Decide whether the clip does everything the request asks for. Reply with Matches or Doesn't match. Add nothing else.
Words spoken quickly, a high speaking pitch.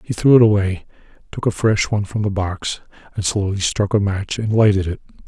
Doesn't match